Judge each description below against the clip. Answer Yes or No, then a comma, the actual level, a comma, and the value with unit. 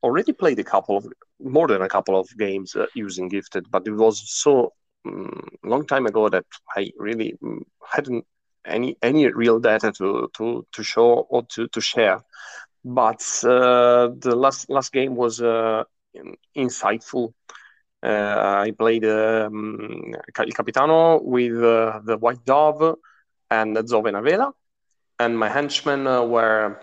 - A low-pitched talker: Yes, low, 120 Hz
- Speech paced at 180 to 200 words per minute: No, average, 145 wpm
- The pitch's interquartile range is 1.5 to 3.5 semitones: Yes, average, 2.9 semitones